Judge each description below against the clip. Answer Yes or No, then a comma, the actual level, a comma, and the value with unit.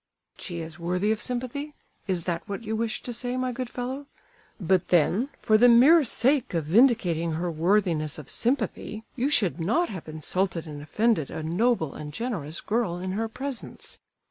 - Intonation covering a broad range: Yes, wide, 6.5 semitones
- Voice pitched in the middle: No, high, 210 Hz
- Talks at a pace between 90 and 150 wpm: No, average, 175 wpm